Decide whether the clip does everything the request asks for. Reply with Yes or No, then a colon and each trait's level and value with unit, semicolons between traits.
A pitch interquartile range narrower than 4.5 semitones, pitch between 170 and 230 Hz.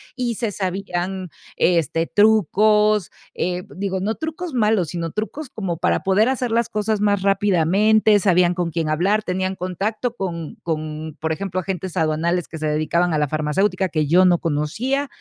Yes: average, 4.1 semitones; medium, 185 Hz